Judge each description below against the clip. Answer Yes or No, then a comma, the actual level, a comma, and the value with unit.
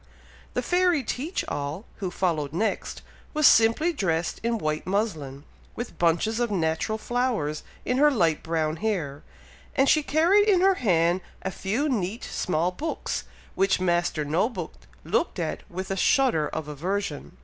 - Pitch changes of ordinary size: No, wide, 7.4 semitones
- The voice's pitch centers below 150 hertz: No, high, 190 Hz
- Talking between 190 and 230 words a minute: No, average, 155 wpm